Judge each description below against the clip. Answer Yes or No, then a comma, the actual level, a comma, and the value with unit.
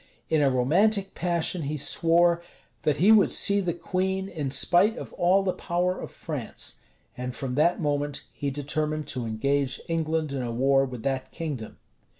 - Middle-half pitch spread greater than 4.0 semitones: Yes, average, 4.4 semitones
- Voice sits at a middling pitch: Yes, medium, 155 Hz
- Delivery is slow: No, average, 170 wpm